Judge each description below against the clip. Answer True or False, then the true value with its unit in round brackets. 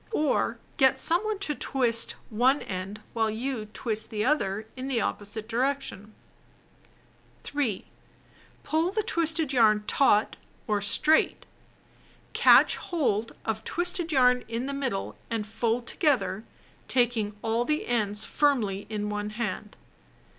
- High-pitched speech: True (235 Hz)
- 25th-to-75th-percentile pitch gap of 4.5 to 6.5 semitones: True (4.8 semitones)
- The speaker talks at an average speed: False (130 wpm)